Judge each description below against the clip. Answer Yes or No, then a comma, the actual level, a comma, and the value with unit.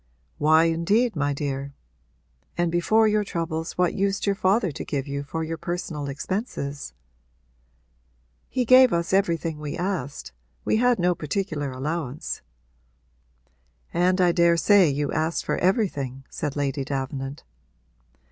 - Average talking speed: No, slow, 130 wpm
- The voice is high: No, medium, 165 Hz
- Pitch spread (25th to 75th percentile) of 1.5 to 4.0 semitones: No, average, 4.9 semitones